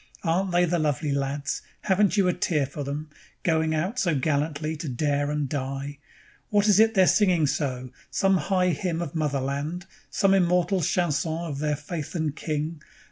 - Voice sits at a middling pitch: Yes, medium, 155 Hz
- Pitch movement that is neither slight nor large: Yes, average, 3.8 semitones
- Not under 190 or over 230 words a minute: No, average, 175 wpm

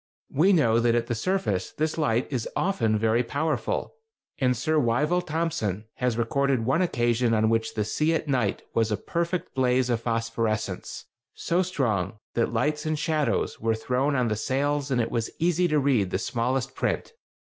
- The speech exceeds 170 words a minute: Yes, average, 180 wpm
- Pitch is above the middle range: No, low, 125 Hz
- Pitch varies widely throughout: No, average, 5.0 semitones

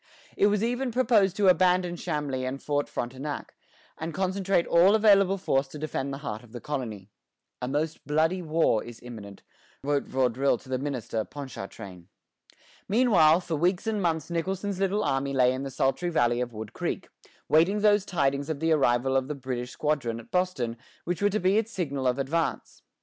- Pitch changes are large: Yes, wide, 6.0 semitones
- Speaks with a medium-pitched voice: Yes, medium, 150 Hz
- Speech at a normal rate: Yes, average, 180 wpm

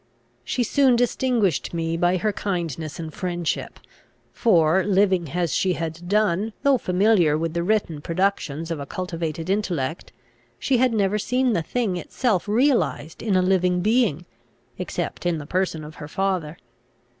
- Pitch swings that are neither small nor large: Yes, average, 4.3 semitones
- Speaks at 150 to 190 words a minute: Yes, average, 155 wpm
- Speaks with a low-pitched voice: No, medium, 180 Hz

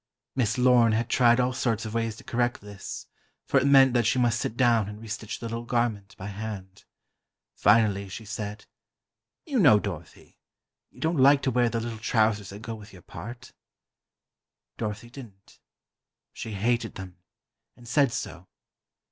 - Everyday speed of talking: Yes, average, 165 wpm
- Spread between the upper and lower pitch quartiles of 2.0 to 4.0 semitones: Yes, average, 2.8 semitones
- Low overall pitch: Yes, low, 115 Hz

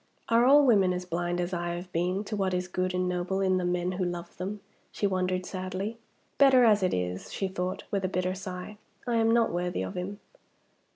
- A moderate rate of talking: No, fast, 220 wpm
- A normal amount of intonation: No, narrow, 2.1 semitones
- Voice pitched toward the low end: No, medium, 185 Hz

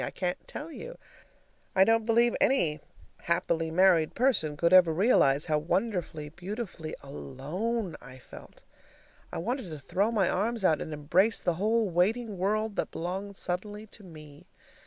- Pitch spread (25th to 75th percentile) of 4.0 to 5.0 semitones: No, wide, 5.4 semitones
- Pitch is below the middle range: No, medium, 185 Hz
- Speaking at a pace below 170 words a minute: Yes, average, 155 wpm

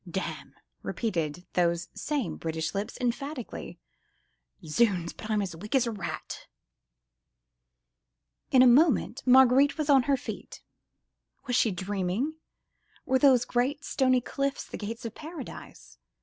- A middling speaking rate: No, slow, 130 wpm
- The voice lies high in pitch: Yes, high, 240 Hz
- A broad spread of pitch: Yes, wide, 5.8 semitones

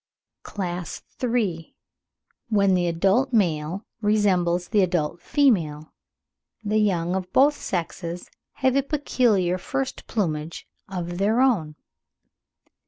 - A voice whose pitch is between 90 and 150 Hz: No, high, 190 Hz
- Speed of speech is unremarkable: No, slow, 110 wpm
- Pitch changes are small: No, average, 4.4 semitones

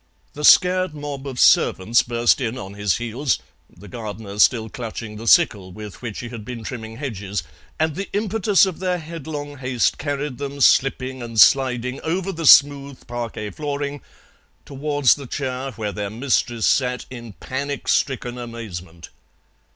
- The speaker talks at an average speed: Yes, average, 155 wpm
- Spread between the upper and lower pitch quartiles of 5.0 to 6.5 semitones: No, average, 4.3 semitones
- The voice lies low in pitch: Yes, low, 125 Hz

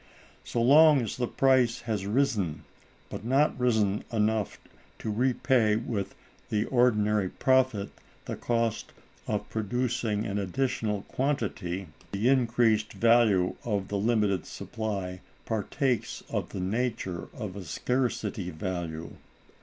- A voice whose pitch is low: Yes, low, 110 Hz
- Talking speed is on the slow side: Yes, slow, 120 wpm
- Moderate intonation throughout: Yes, average, 3.7 semitones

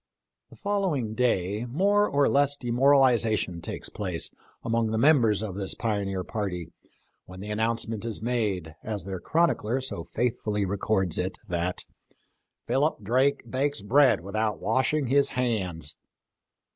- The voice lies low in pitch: Yes, low, 110 Hz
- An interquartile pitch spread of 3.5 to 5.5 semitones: Yes, average, 5.1 semitones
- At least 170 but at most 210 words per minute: No, slow, 135 wpm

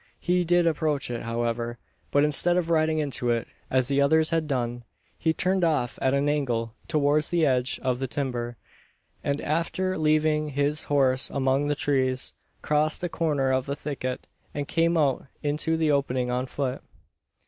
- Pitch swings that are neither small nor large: Yes, average, 3.3 semitones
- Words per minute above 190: No, average, 170 wpm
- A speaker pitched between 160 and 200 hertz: No, medium, 145 Hz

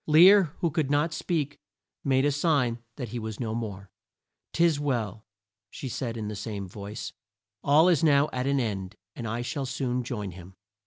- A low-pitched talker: Yes, low, 125 Hz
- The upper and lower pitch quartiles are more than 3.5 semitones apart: Yes, average, 5.1 semitones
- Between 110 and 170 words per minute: No, average, 180 wpm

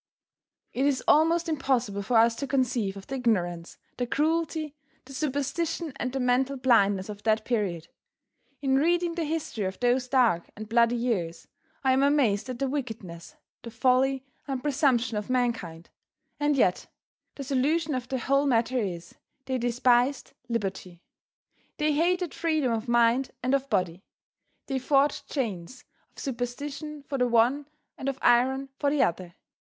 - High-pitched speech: Yes, very high, 255 Hz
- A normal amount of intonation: Yes, average, 3.7 semitones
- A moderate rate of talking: Yes, average, 155 wpm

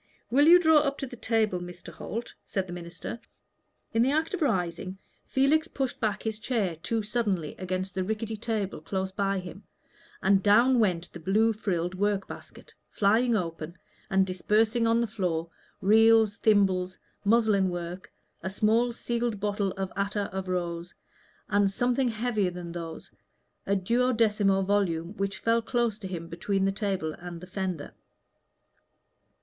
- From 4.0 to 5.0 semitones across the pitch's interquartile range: No, average, 3.6 semitones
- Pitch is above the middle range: Yes, high, 200 Hz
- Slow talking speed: No, average, 155 wpm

